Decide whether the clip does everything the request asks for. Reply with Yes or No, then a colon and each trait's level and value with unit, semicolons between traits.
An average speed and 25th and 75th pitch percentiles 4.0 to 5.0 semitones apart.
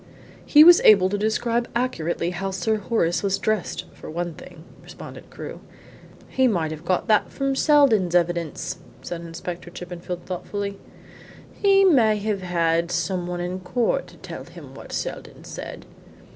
Yes: average, 155 wpm; average, 4.3 semitones